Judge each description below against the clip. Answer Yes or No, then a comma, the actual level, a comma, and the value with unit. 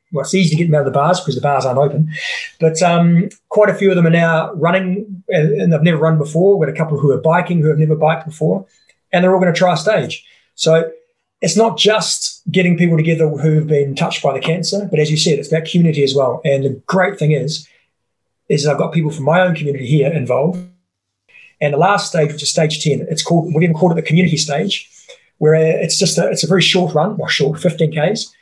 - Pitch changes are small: No, average, 3.2 semitones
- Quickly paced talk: Yes, fast, 250 wpm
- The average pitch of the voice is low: No, medium, 165 Hz